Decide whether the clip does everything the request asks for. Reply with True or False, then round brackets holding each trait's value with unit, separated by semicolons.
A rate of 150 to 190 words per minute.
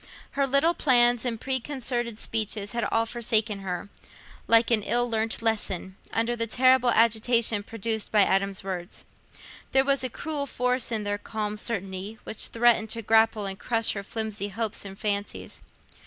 True (160 wpm)